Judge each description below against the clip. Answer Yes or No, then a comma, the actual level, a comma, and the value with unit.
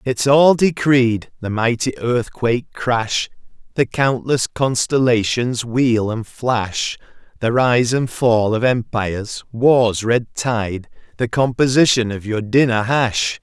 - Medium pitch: No, low, 120 Hz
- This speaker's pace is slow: Yes, slow, 125 wpm